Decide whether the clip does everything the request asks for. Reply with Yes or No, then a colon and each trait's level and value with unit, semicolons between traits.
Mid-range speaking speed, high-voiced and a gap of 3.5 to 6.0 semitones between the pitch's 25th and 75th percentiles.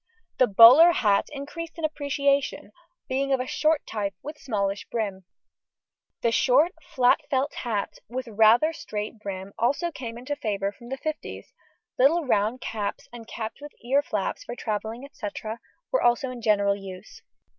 Yes: average, 155 wpm; high, 240 Hz; average, 5.0 semitones